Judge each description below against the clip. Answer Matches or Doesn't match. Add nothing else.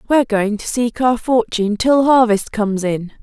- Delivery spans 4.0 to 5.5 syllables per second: Matches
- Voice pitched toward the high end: Matches